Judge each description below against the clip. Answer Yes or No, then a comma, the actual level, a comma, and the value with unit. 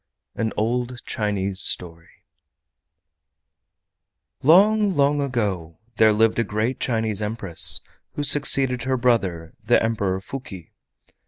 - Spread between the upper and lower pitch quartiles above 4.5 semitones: Yes, average, 5.0 semitones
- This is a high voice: No, low, 115 Hz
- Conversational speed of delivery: No, slow, 105 wpm